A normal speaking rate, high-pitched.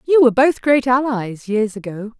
Yes: average, 190 wpm; high, 240 Hz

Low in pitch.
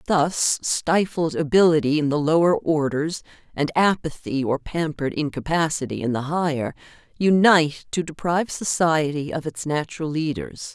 No: medium, 155 Hz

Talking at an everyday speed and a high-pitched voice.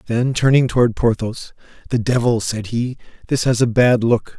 No: average, 180 wpm; low, 120 Hz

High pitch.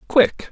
Yes: very high, 270 Hz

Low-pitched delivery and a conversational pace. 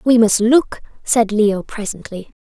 No: high, 220 Hz; average, 150 wpm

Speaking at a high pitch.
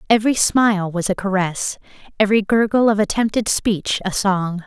Yes: high, 205 Hz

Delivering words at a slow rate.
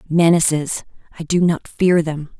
Yes: slow, 125 wpm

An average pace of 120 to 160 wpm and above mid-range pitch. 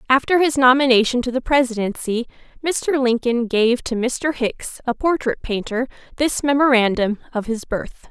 Yes: average, 150 wpm; very high, 250 Hz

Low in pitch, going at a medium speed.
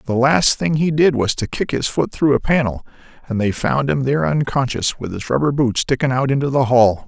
No: low, 130 Hz; fast, 235 wpm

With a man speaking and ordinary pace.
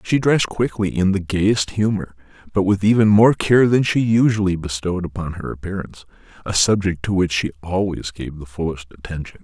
Yes: male; average, 185 wpm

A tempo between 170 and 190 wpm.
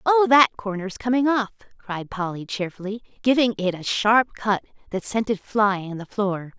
Yes: average, 180 wpm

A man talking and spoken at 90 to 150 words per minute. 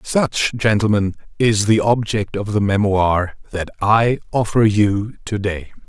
Yes: male; average, 145 wpm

